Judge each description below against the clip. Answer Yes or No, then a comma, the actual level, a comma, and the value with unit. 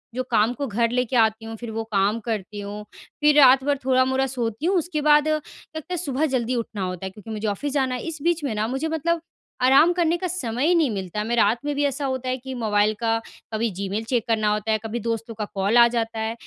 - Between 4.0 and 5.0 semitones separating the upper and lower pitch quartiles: Yes, average, 4.7 semitones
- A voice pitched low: No, high, 240 Hz